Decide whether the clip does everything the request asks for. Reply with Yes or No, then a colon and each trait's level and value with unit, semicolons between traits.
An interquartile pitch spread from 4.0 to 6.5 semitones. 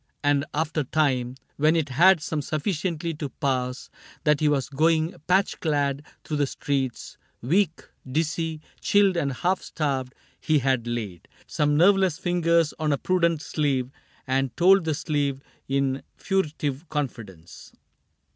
No: average, 3.5 semitones